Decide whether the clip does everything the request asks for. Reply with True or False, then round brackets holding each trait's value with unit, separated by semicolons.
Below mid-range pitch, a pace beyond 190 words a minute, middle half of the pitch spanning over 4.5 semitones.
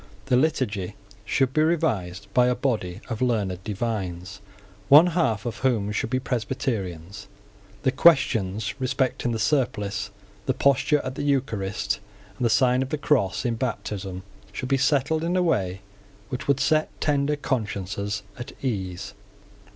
False (120 Hz; 150 wpm; 5.3 semitones)